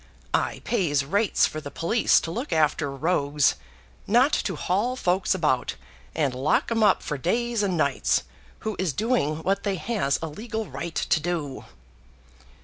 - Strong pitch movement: Yes, wide, 6.5 semitones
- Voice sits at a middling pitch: Yes, medium, 175 Hz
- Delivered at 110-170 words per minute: Yes, average, 160 wpm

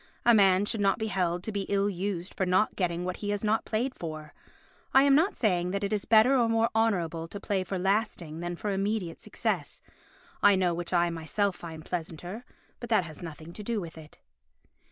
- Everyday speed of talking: No, fast, 215 wpm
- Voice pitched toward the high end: Yes, high, 195 Hz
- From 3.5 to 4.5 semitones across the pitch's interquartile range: Yes, average, 3.8 semitones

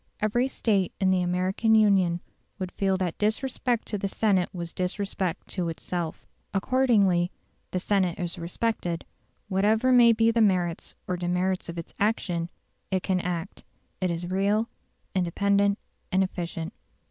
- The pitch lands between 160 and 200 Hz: Yes, high, 190 Hz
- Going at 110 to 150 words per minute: Yes, average, 145 wpm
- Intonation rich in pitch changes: No, average, 3.0 semitones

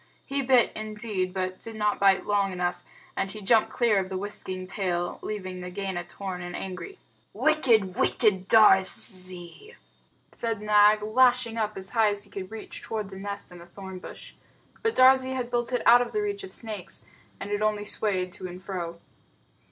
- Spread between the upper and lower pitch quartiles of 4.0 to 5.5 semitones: No, average, 3.6 semitones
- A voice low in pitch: No, high, 205 Hz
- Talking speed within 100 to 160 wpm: No, average, 180 wpm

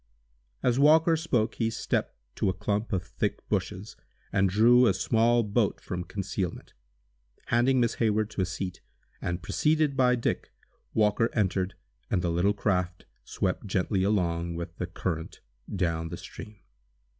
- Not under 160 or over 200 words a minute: No, average, 150 wpm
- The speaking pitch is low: Yes, low, 100 Hz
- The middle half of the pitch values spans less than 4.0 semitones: No, average, 4.3 semitones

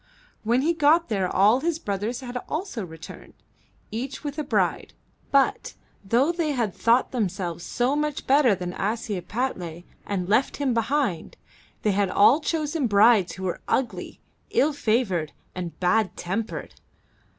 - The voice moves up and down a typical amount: No, wide, 6.6 semitones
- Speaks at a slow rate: No, average, 145 wpm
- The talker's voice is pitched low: No, high, 230 Hz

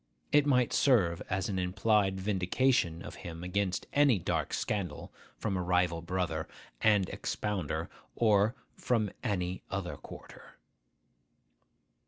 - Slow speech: Yes, slow, 120 wpm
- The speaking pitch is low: Yes, very low, 95 Hz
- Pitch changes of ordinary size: Yes, average, 3.3 semitones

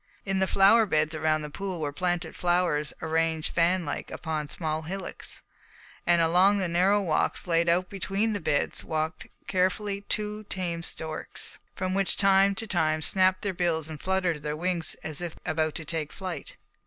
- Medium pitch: Yes, medium, 175 Hz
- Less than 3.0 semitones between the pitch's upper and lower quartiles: No, average, 3.3 semitones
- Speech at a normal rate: Yes, average, 170 wpm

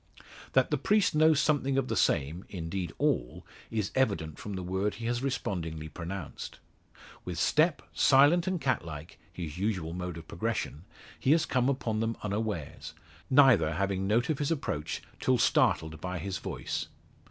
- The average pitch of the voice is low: Yes, low, 100 Hz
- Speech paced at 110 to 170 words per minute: Yes, average, 165 wpm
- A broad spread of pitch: Yes, wide, 8.0 semitones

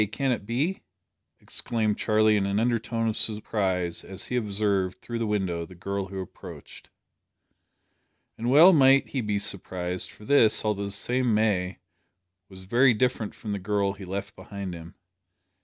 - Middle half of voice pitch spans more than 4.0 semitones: No, average, 3.2 semitones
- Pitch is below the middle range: Yes, low, 105 Hz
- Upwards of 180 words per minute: No, average, 160 wpm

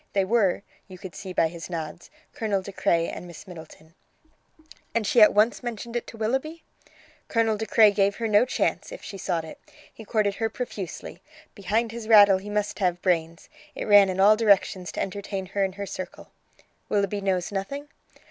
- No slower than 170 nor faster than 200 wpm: Yes, average, 190 wpm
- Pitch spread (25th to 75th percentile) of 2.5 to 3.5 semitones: Yes, average, 3.0 semitones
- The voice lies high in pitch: Yes, high, 200 Hz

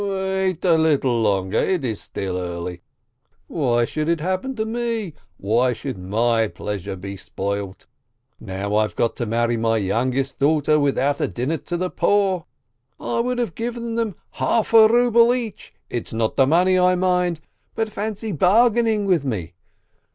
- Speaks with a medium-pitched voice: Yes, medium, 155 Hz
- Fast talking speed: No, average, 160 wpm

